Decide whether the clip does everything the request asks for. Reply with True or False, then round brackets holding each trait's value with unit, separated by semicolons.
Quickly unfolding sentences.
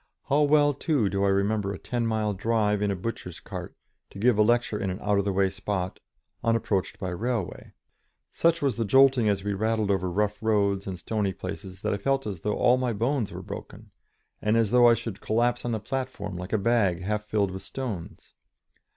True (210 wpm)